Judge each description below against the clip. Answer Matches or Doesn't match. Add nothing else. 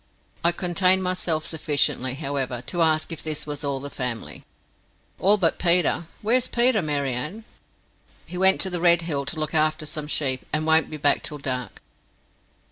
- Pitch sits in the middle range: Matches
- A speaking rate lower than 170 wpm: Doesn't match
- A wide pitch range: Doesn't match